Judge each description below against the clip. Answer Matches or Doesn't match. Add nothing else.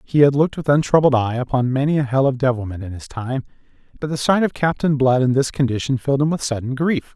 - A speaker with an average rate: Doesn't match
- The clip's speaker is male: Matches